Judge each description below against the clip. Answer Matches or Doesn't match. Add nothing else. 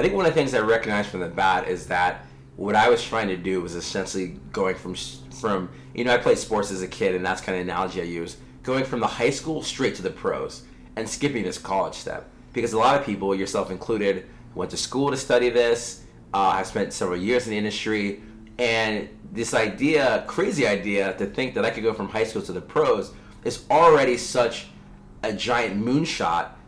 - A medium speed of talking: Doesn't match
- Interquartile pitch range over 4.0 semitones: Matches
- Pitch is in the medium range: Doesn't match